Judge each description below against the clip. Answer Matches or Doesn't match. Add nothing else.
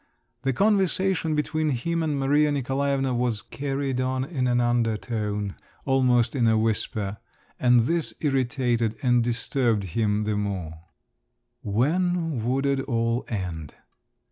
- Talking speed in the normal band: Doesn't match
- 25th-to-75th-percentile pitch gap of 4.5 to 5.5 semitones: Doesn't match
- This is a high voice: Doesn't match